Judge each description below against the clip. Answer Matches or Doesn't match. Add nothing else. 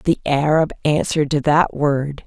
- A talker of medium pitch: Matches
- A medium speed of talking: Matches